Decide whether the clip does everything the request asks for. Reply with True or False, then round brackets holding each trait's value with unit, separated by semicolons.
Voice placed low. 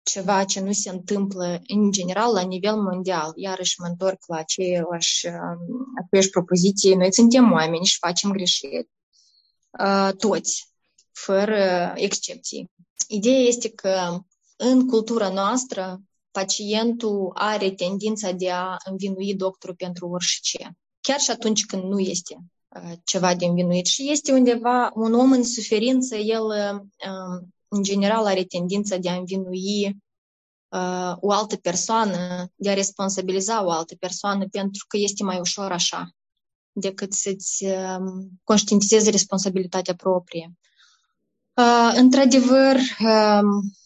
False (195 Hz)